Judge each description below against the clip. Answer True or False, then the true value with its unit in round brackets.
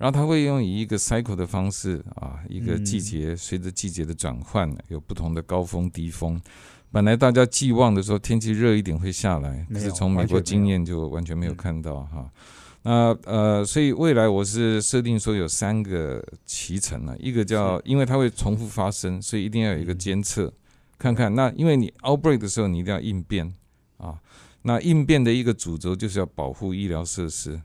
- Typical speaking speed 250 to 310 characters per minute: False (320 characters per minute)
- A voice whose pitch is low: True (100 Hz)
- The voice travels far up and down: False (4.6 semitones)